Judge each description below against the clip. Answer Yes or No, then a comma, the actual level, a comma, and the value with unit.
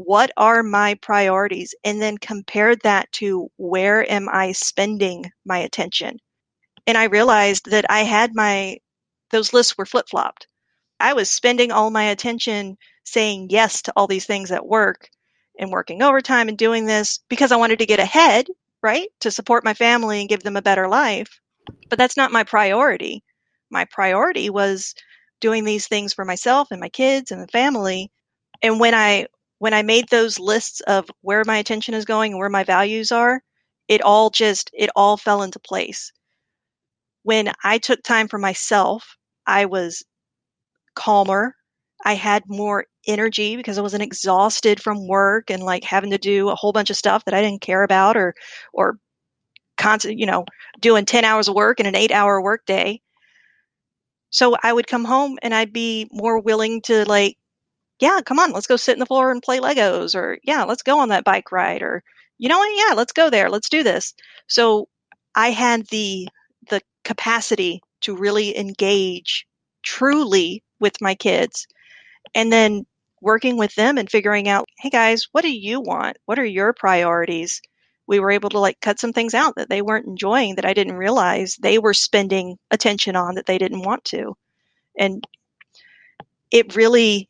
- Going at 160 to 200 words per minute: Yes, average, 180 wpm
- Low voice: No, high, 215 Hz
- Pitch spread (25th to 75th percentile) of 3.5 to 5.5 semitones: No, average, 2.7 semitones